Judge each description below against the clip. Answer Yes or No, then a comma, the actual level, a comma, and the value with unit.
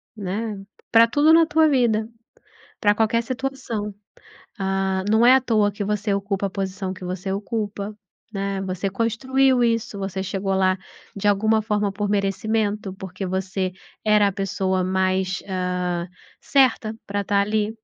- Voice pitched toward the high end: Yes, high, 205 Hz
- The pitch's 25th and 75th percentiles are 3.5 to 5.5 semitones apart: No, narrow, 2.5 semitones